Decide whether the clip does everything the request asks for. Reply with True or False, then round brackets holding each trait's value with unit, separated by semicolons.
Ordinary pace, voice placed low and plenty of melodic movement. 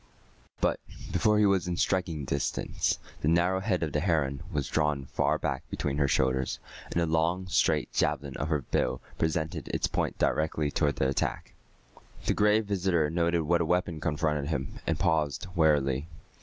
False (170 wpm; 80 Hz; 3.2 semitones)